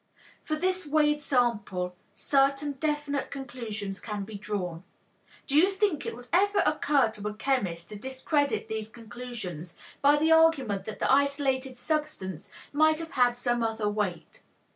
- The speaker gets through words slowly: No, average, 150 wpm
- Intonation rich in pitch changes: Yes, wide, 5.9 semitones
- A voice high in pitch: Yes, very high, 255 Hz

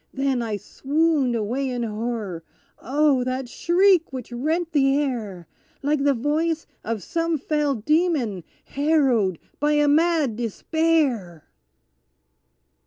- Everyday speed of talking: No, slow, 115 wpm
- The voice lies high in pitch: Yes, very high, 275 Hz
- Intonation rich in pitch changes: No, average, 4.8 semitones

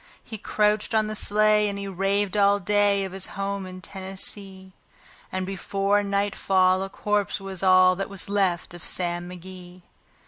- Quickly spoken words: No, average, 165 wpm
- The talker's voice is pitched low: No, high, 195 Hz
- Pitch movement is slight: Yes, narrow, 1.6 semitones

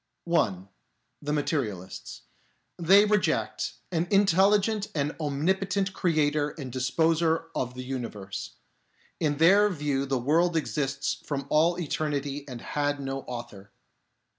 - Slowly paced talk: Yes, slow, 120 wpm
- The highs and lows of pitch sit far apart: No, average, 4.3 semitones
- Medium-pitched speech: Yes, medium, 150 Hz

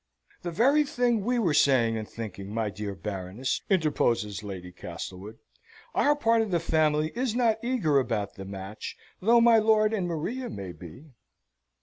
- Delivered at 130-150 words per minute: No, average, 160 wpm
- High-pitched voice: No, medium, 150 Hz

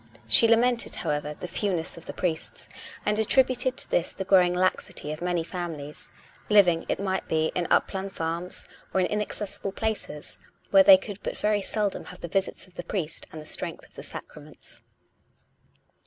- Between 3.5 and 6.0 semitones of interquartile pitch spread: Yes, average, 3.9 semitones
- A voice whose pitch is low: No, medium, 185 Hz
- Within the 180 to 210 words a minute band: Yes, average, 185 wpm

